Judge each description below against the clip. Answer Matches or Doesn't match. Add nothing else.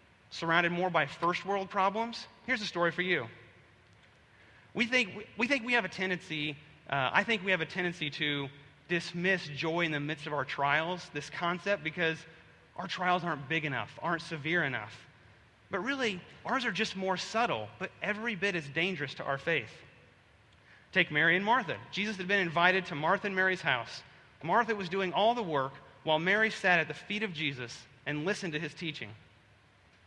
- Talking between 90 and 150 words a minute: Doesn't match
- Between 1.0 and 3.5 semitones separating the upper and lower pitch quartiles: Doesn't match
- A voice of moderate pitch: Matches